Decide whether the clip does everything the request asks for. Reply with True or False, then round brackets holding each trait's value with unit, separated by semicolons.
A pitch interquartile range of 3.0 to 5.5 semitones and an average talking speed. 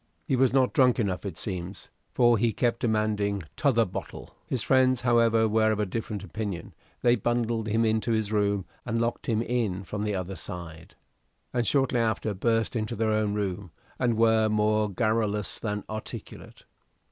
False (2.4 semitones; 170 wpm)